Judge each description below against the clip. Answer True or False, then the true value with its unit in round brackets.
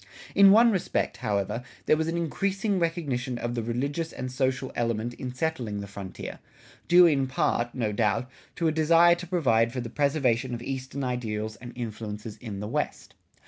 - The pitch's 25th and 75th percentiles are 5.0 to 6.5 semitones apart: True (5.6 semitones)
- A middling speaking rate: True (180 wpm)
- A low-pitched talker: True (125 Hz)